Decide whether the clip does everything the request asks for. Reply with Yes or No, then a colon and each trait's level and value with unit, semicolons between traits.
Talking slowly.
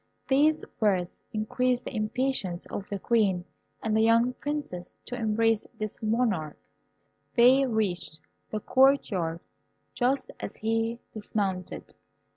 Yes: slow, 120 wpm